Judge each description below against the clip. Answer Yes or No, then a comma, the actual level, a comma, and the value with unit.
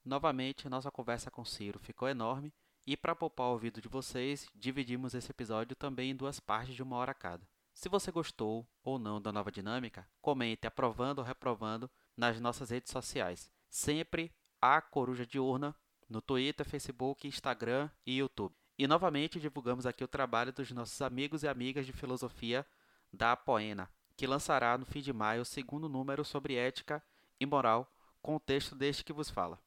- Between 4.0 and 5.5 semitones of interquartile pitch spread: No, average, 3.1 semitones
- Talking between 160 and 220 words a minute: Yes, average, 180 wpm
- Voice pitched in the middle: No, low, 130 Hz